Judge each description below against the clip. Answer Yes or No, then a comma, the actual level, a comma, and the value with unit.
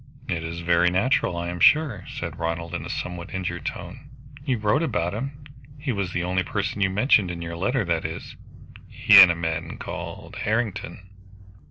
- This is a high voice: No, very low, 90 Hz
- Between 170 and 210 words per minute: Yes, average, 185 wpm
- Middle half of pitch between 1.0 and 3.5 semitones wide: No, average, 4.0 semitones